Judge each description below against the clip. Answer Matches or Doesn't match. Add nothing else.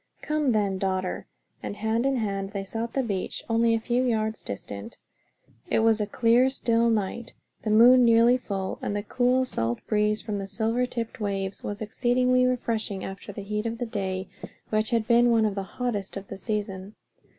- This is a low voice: Doesn't match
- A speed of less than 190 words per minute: Doesn't match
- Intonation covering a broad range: Doesn't match